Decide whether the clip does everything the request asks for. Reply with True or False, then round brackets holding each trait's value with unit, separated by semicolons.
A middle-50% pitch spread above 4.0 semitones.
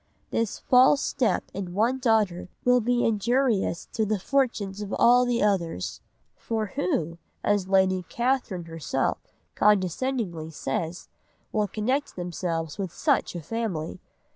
True (5.2 semitones)